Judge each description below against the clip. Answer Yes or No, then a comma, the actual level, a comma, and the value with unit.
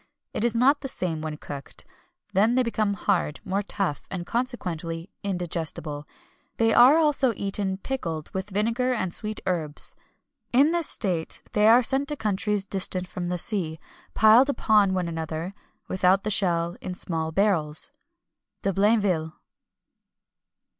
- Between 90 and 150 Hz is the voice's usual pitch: No, high, 195 Hz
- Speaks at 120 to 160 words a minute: Yes, average, 150 wpm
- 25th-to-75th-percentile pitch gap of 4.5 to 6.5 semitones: Yes, average, 5.0 semitones